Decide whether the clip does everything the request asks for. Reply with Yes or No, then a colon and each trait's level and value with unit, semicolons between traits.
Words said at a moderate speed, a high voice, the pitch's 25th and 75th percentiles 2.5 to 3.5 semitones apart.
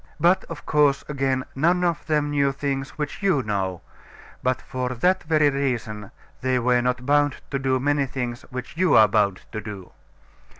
No: average, 175 wpm; low, 135 Hz; average, 3.1 semitones